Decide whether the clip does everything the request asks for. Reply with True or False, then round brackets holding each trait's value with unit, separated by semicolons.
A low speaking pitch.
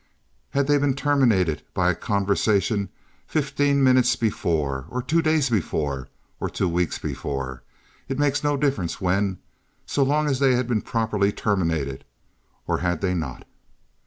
True (105 Hz)